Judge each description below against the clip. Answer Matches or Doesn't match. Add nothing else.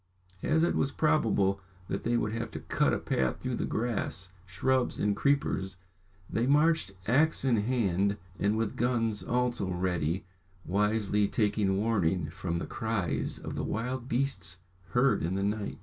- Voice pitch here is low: Matches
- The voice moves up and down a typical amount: Matches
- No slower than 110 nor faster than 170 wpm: Matches